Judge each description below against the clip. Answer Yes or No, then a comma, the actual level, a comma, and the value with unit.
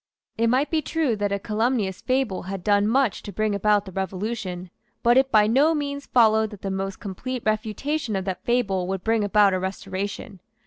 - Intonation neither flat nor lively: Yes, average, 3.8 semitones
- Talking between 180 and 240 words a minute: Yes, average, 195 wpm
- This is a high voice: Yes, high, 210 Hz